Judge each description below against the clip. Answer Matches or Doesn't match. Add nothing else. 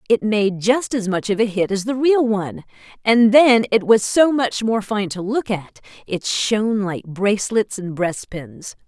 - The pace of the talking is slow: Doesn't match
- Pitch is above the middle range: Matches